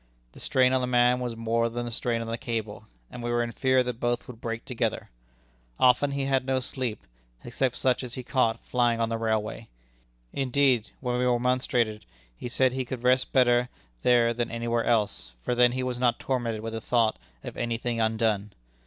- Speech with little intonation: Yes, narrow, 1.7 semitones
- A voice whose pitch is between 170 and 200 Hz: No, low, 120 Hz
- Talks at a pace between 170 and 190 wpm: No, fast, 205 wpm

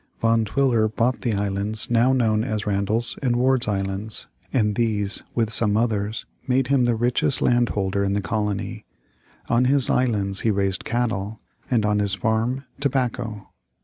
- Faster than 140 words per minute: Yes, average, 160 wpm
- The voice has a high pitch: No, low, 110 Hz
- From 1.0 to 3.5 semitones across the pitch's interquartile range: Yes, average, 2.9 semitones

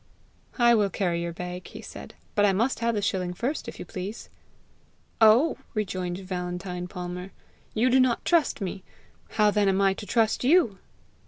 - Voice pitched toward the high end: Yes, high, 195 Hz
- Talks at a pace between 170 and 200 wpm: Yes, average, 175 wpm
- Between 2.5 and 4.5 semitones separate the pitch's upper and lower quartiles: Yes, average, 4.2 semitones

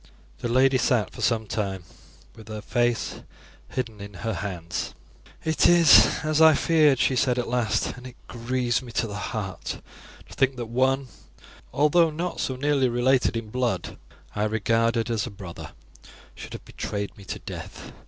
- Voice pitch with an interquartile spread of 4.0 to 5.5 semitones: No, average, 3.5 semitones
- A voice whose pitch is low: Yes, low, 120 Hz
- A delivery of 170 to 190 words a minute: Yes, average, 175 wpm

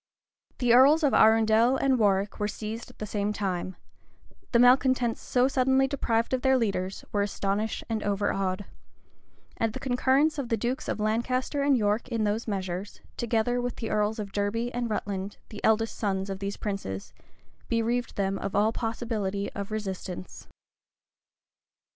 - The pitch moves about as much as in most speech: Yes, average, 3.4 semitones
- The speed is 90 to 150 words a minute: No, average, 160 wpm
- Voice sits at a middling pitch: No, high, 220 Hz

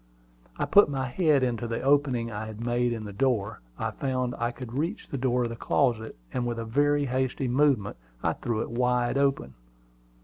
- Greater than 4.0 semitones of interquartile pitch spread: No, average, 2.8 semitones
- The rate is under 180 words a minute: No, average, 200 wpm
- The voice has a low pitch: Yes, low, 125 Hz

